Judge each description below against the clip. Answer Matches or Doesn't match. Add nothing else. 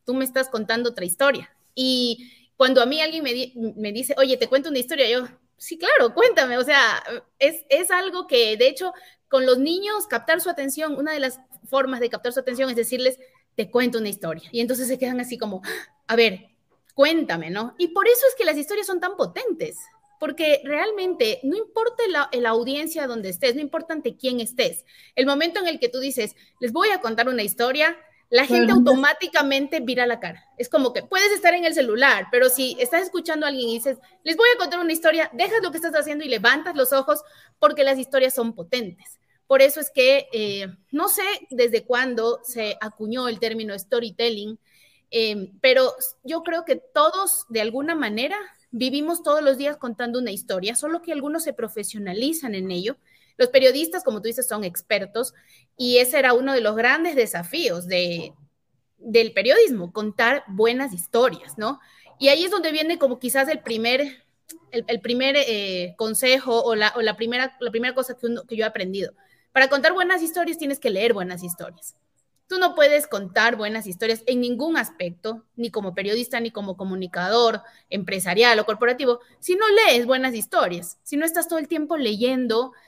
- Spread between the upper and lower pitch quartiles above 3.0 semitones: Matches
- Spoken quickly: Matches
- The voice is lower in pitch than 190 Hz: Doesn't match